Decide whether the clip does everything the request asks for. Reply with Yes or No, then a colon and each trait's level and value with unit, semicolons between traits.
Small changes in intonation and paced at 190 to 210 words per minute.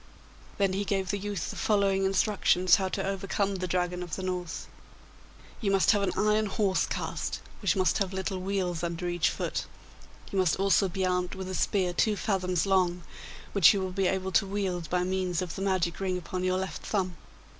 Yes: narrow, 1.4 semitones; average, 200 wpm